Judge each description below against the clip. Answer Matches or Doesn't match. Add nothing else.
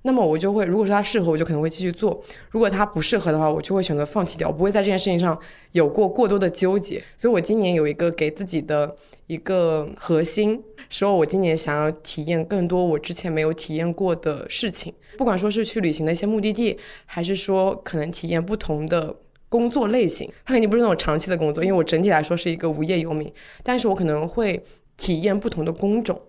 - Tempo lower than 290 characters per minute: Doesn't match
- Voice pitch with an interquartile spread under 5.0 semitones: Matches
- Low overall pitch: Doesn't match